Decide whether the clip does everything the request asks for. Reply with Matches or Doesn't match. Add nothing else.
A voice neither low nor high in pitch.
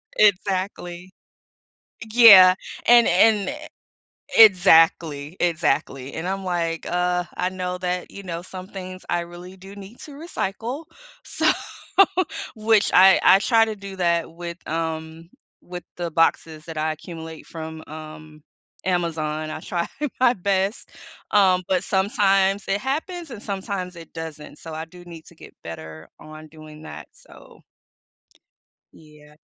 Matches